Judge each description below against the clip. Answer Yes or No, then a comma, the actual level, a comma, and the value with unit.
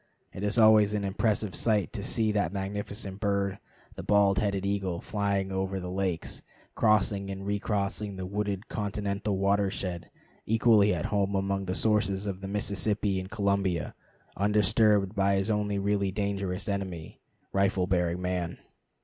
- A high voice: No, low, 100 Hz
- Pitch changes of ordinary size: No, narrow, 1.2 semitones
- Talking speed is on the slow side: No, average, 150 wpm